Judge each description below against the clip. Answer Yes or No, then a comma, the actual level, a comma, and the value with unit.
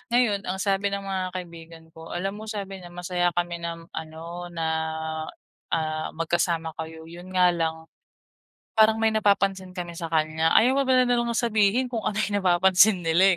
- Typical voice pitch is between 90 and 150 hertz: No, medium, 180 Hz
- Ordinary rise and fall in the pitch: Yes, average, 3.5 semitones